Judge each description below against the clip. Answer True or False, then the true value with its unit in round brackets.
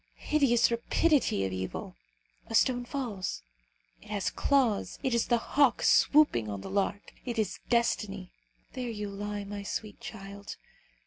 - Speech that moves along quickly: False (145 wpm)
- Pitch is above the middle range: True (215 Hz)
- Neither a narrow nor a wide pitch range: True (3.5 semitones)